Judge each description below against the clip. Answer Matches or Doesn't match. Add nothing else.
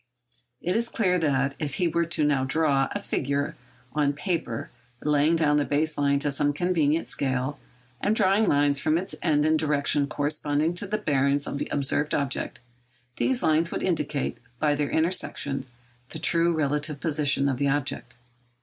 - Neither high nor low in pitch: Matches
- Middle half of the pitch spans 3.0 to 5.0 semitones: Doesn't match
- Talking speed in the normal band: Matches